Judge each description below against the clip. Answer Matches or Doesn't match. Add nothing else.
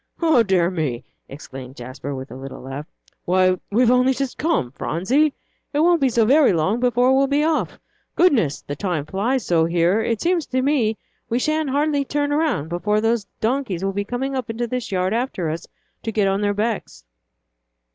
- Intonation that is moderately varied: Doesn't match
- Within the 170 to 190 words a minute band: Matches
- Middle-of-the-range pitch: Doesn't match